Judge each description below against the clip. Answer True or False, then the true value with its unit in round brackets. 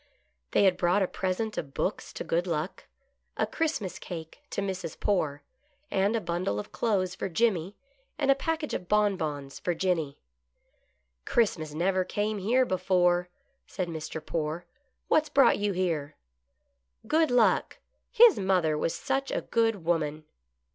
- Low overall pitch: False (185 Hz)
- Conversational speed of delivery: True (160 wpm)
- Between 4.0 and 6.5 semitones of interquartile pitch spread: True (4.8 semitones)